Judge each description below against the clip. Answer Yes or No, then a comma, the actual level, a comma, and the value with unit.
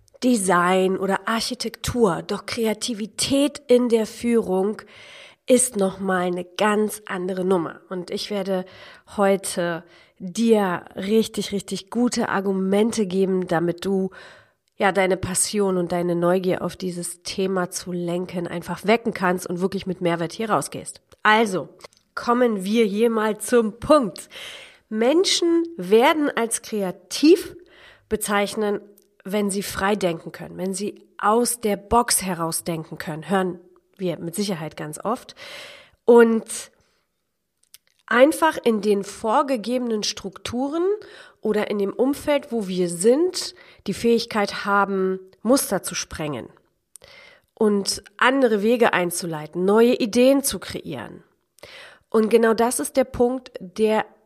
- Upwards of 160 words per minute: No, slow, 125 wpm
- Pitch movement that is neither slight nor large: Yes, average, 3.9 semitones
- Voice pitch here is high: Yes, high, 205 Hz